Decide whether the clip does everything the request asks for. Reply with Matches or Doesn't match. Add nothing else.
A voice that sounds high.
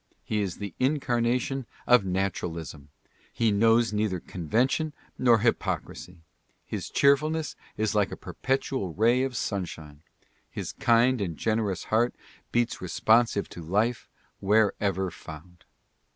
Doesn't match